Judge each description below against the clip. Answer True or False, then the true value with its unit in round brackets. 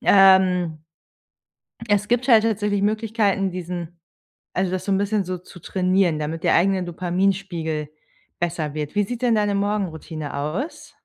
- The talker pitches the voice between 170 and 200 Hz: True (190 Hz)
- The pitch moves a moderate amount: True (3.1 semitones)